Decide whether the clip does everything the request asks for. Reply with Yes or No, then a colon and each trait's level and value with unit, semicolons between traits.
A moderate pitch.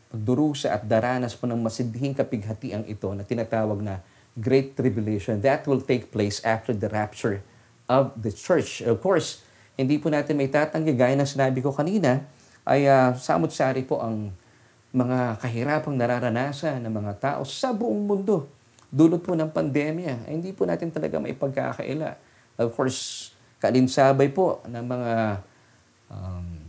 No: low, 125 Hz